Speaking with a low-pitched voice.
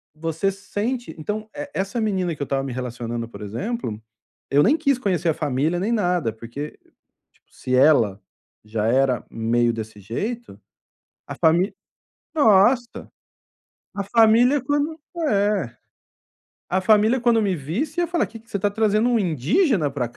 No: high, 190 Hz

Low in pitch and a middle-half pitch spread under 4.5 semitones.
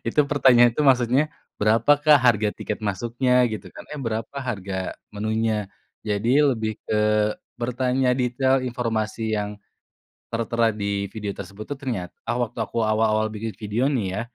Yes: low, 115 Hz; average, 2.8 semitones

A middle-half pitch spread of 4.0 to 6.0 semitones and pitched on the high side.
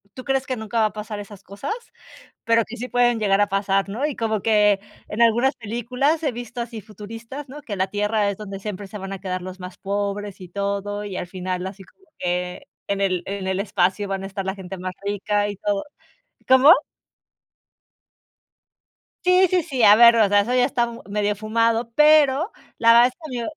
No: average, 3.3 semitones; high, 210 Hz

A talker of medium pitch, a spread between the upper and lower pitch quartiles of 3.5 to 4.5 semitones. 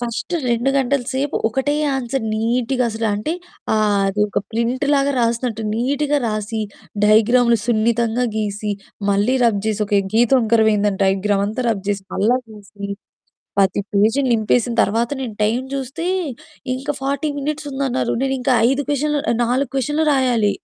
No: high, 235 Hz; average, 3.8 semitones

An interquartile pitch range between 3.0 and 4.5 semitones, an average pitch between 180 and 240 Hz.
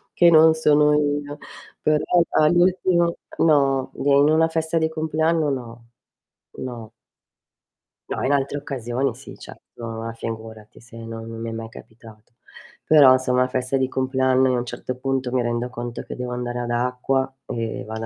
No: average, 3.8 semitones; low, 130 Hz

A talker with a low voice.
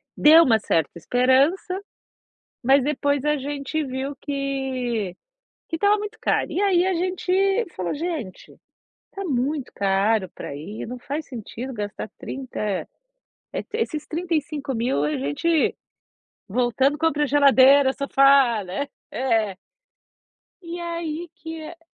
No: very high, 275 Hz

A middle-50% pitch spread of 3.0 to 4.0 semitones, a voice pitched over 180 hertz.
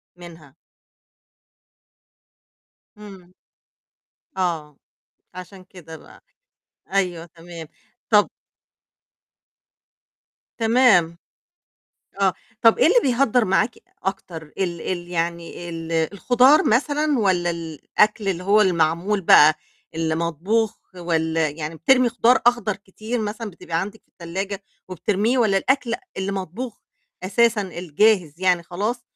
No: average, 4.4 semitones; high, 190 Hz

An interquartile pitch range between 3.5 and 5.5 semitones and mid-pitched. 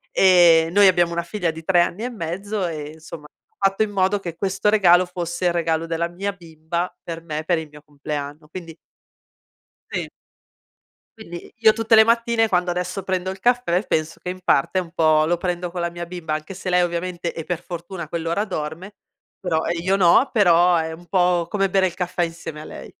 No: narrow, 2.4 semitones; medium, 175 Hz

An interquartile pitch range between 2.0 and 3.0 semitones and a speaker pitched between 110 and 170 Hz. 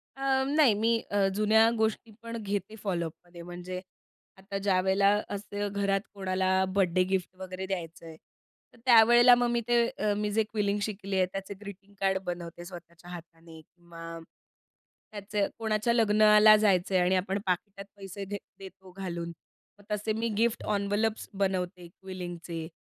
No: average, 2.7 semitones; high, 195 Hz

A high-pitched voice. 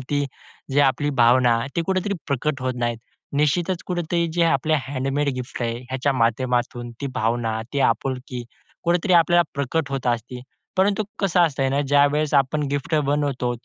No: medium, 140 Hz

